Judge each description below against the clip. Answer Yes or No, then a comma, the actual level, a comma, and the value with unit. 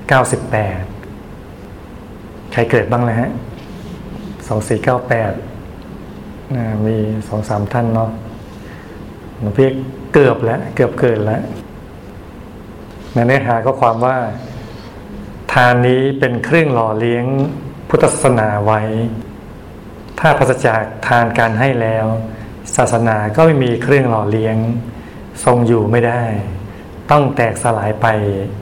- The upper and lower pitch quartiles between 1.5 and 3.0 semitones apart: Yes, narrow, 2.6 semitones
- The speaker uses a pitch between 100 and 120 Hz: Yes, low, 115 Hz